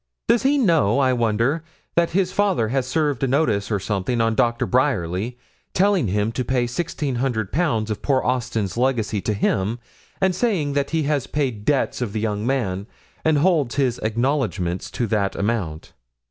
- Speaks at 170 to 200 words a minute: Yes, average, 175 wpm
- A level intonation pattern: No, wide, 5.4 semitones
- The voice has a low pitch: Yes, low, 125 Hz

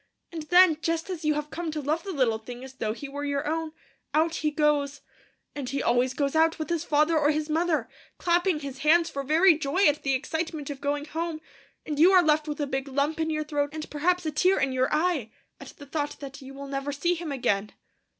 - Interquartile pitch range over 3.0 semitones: No, narrow, 2.6 semitones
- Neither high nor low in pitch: No, very high, 300 Hz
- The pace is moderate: No, fast, 235 wpm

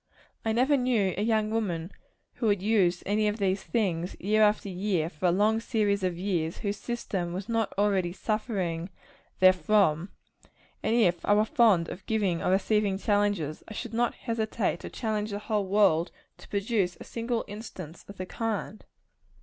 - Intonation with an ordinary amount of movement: Yes, average, 3.1 semitones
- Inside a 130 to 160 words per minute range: No, average, 175 wpm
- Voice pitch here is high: Yes, high, 205 Hz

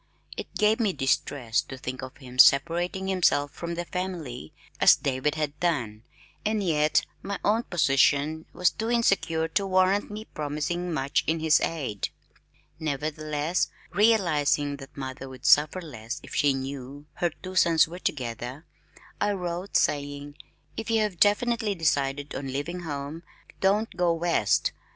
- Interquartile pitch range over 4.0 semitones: Yes, average, 4.7 semitones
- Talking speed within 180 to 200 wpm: No, average, 150 wpm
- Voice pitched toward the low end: No, medium, 155 Hz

